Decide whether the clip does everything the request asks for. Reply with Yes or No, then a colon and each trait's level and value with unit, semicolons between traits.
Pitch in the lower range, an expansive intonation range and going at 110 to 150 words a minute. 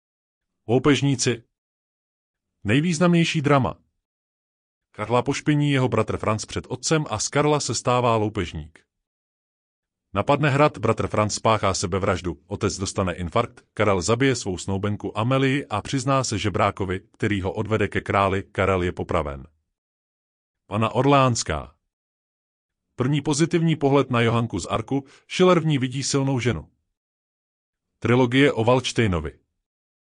Yes: low, 110 Hz; wide, 6.1 semitones; average, 120 wpm